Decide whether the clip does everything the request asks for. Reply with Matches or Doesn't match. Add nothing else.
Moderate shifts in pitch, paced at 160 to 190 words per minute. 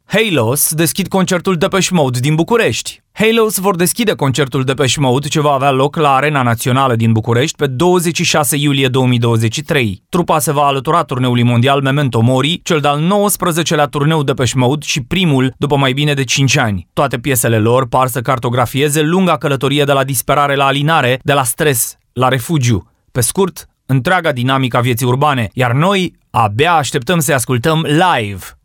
Matches